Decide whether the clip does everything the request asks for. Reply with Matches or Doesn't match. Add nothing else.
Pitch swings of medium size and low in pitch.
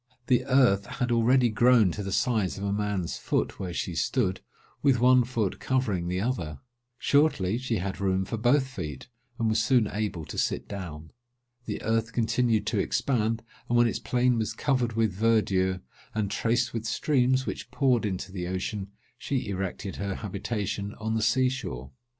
Matches